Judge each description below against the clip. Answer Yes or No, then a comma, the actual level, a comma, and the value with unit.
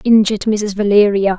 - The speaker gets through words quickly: No, slow, 130 wpm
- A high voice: Yes, high, 205 Hz